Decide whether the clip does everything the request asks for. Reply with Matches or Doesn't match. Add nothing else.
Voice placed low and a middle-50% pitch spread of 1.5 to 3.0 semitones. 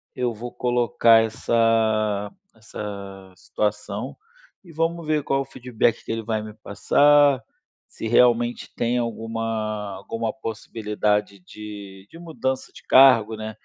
Matches